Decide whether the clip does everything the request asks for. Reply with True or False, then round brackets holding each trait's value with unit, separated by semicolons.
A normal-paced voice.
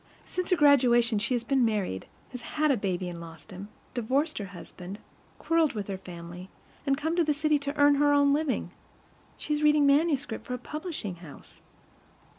True (190 wpm)